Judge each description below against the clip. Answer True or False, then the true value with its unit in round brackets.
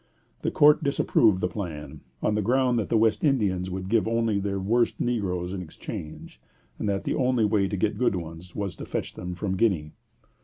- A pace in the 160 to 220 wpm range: True (200 wpm)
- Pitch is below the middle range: True (100 Hz)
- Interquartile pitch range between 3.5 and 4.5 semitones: True (4.0 semitones)